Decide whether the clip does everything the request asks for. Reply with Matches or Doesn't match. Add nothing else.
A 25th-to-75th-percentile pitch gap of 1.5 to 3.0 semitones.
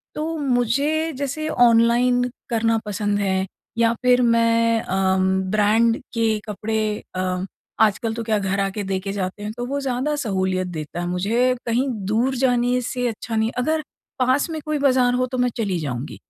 Doesn't match